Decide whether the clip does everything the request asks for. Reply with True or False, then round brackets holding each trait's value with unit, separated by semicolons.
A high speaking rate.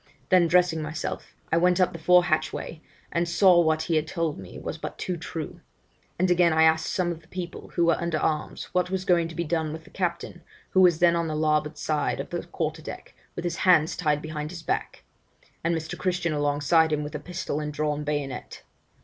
True (220 wpm)